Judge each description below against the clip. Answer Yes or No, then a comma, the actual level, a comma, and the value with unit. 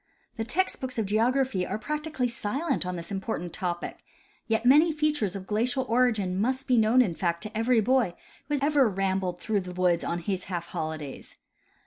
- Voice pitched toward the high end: Yes, high, 220 Hz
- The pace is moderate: Yes, average, 180 wpm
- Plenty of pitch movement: Yes, wide, 5.9 semitones